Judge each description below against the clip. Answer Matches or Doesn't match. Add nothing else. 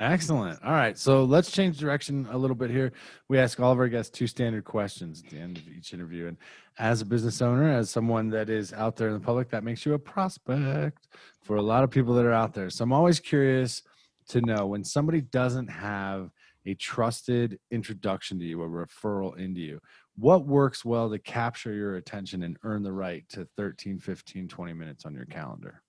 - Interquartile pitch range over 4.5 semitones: Matches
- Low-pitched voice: Matches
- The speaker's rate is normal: Doesn't match